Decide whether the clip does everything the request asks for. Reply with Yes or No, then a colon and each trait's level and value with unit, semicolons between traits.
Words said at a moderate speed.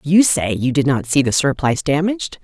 No: fast, 220 wpm